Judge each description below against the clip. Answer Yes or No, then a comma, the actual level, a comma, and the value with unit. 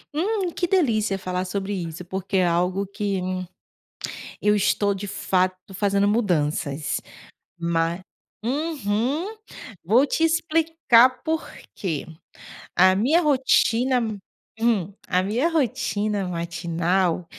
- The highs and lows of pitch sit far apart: Yes, wide, 6.2 semitones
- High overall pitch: Yes, high, 200 Hz